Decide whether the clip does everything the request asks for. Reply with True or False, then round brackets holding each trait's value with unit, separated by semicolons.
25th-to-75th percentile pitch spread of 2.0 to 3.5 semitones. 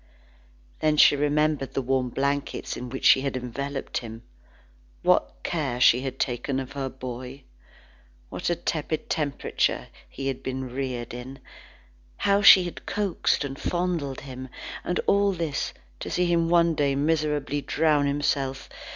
True (2.9 semitones)